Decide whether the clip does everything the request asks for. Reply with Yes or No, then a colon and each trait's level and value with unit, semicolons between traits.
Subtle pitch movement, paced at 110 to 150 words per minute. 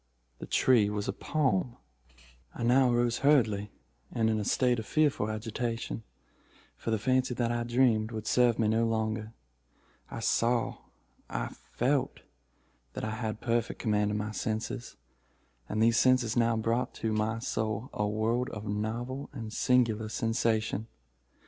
Yes: narrow, 2.0 semitones; average, 140 wpm